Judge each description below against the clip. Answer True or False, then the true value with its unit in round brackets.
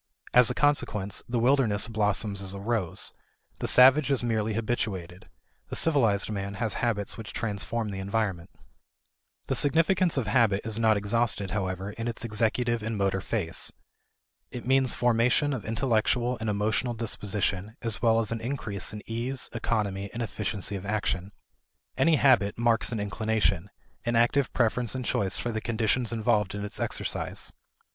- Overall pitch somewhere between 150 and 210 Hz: False (110 Hz)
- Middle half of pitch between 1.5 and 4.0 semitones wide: True (2.7 semitones)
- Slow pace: False (160 wpm)